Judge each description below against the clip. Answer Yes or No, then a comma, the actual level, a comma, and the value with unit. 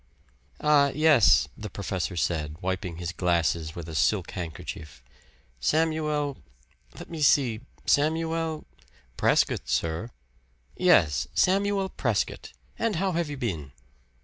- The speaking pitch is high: No, low, 110 Hz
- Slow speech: Yes, slow, 120 wpm